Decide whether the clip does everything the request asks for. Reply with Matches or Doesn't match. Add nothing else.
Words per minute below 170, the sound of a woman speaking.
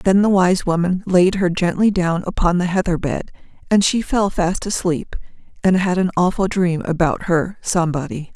Doesn't match